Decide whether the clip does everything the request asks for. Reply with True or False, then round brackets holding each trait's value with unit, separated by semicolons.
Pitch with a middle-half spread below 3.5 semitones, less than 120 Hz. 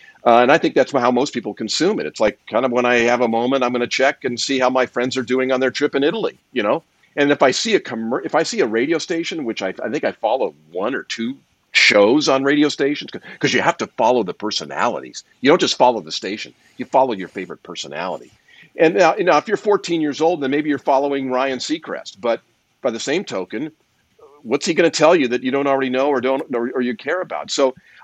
False (2.9 semitones; 135 Hz)